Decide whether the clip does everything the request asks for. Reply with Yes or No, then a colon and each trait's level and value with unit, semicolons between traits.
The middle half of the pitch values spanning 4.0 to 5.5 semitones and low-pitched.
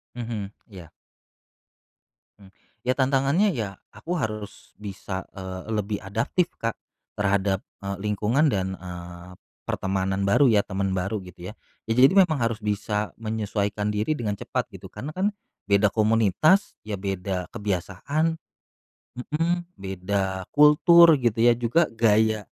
Yes: average, 4.5 semitones; low, 105 Hz